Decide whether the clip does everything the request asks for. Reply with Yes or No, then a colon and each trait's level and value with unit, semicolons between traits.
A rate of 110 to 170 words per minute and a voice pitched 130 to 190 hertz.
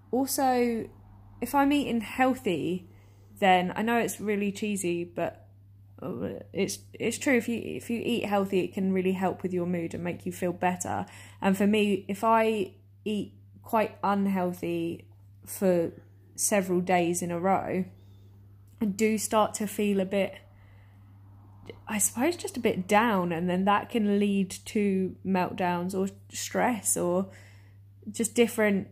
Yes: average, 150 wpm; medium, 185 Hz